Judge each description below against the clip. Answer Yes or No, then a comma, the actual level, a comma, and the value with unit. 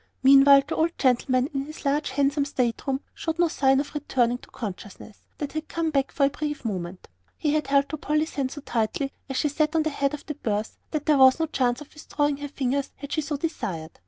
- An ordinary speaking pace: No, fast, 240 wpm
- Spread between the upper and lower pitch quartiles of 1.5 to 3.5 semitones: Yes, narrow, 2.6 semitones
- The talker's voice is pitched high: Yes, very high, 280 Hz